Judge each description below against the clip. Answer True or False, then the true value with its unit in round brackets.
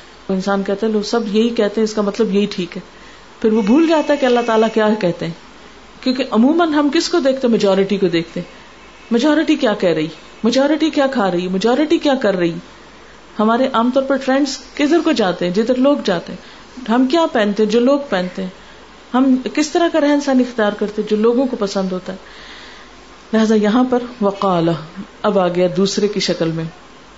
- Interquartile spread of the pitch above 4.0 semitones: True (5.2 semitones)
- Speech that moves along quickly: True (210 wpm)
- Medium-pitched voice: False (220 Hz)